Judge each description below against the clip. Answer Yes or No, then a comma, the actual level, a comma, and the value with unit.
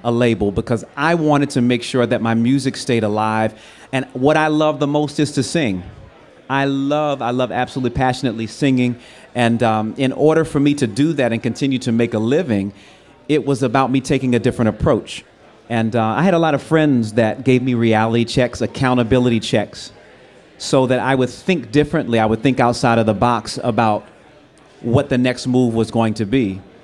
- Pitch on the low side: Yes, low, 125 Hz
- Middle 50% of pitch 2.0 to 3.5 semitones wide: Yes, average, 3.1 semitones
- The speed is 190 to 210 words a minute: Yes, average, 200 wpm